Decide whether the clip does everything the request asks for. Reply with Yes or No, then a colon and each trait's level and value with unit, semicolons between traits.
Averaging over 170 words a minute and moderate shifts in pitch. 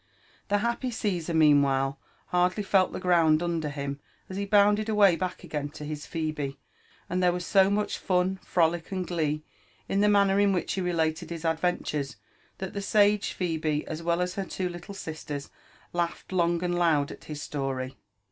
Yes: average, 185 wpm; average, 3.9 semitones